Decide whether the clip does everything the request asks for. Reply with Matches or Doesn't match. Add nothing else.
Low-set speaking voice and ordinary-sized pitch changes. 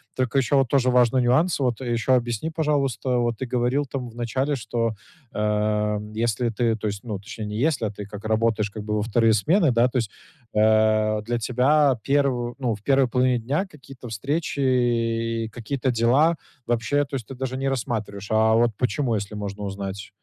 Matches